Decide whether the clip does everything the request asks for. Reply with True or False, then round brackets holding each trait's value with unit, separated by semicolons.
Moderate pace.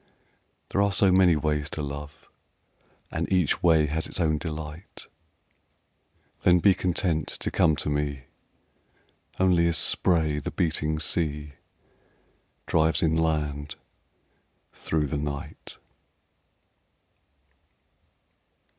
False (100 wpm)